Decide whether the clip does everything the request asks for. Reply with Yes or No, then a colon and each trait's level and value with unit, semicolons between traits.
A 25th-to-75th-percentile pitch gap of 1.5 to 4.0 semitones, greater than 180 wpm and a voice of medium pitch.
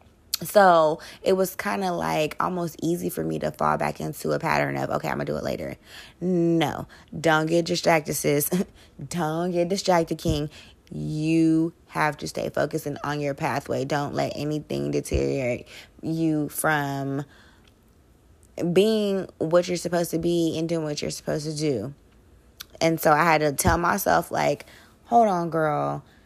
No: average, 3.2 semitones; average, 160 wpm; medium, 155 Hz